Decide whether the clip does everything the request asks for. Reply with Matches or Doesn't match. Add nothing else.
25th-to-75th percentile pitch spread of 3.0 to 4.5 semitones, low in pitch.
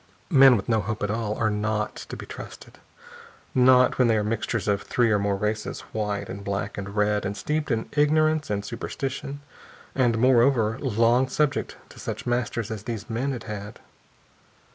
Matches